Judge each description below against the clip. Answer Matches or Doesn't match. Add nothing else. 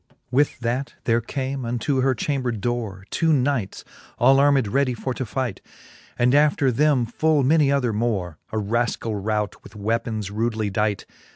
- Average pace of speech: Matches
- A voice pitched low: Matches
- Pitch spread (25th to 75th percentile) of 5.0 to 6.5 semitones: Doesn't match